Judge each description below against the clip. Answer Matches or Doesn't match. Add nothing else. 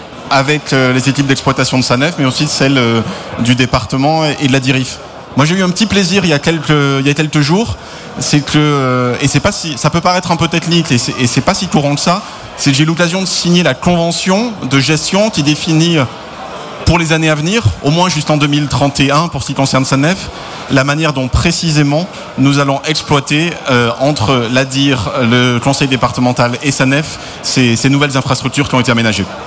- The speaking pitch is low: Doesn't match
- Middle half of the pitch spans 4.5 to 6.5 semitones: Doesn't match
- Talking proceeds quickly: Doesn't match